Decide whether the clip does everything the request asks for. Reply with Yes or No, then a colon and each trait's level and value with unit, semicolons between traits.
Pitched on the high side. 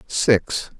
No: low, 115 Hz